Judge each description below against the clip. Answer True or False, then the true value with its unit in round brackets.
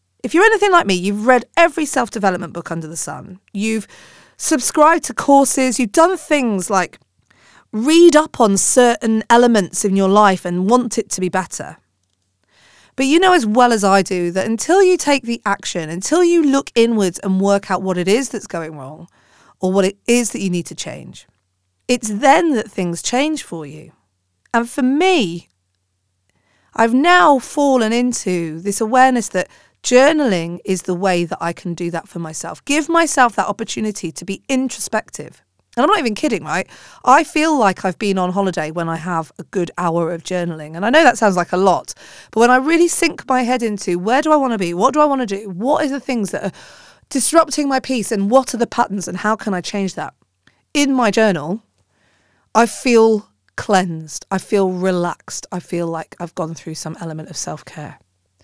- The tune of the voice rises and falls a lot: True (6.7 semitones)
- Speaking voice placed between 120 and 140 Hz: False (205 Hz)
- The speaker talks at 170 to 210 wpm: True (200 wpm)